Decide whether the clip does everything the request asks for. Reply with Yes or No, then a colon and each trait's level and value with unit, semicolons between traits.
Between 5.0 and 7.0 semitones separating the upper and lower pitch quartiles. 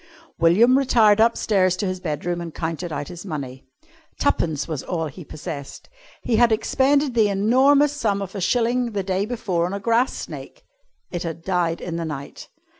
Yes: wide, 5.6 semitones